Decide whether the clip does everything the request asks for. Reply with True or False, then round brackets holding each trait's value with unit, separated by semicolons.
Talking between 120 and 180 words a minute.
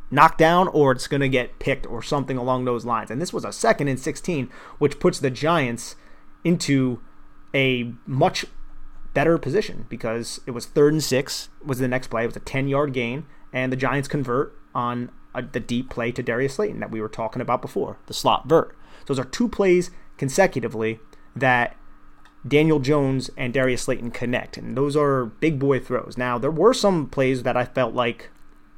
False (195 wpm)